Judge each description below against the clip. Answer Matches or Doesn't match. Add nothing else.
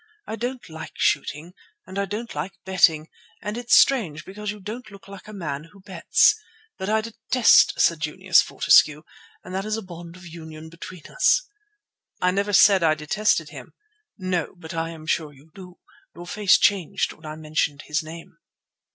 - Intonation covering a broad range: Doesn't match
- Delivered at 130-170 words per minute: Doesn't match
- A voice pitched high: Doesn't match